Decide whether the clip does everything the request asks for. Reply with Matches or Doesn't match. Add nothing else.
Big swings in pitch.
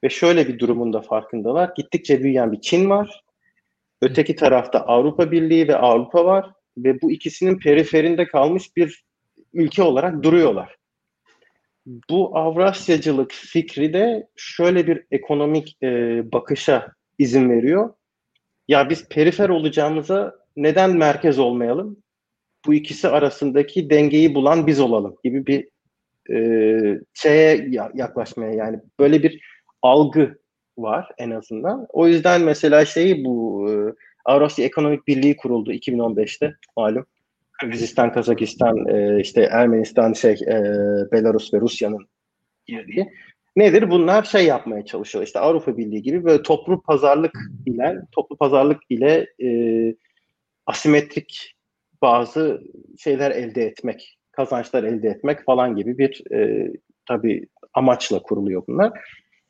Matches